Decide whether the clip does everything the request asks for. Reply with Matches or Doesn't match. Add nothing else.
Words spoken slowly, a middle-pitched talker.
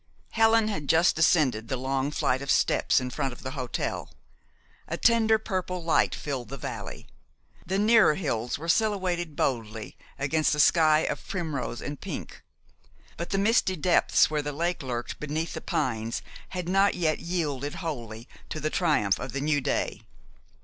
Doesn't match